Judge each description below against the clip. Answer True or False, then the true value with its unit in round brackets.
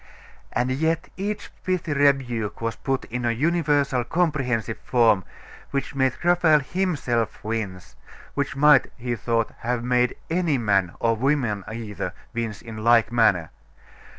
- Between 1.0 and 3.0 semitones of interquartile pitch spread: False (4.3 semitones)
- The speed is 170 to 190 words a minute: False (135 wpm)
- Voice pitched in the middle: False (125 Hz)